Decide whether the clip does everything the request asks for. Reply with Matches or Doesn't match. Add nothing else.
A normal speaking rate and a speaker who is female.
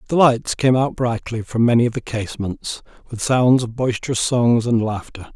Doesn't match